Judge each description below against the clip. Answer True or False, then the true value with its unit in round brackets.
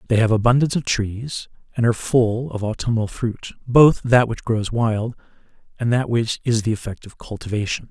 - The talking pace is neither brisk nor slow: True (180 wpm)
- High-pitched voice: False (115 Hz)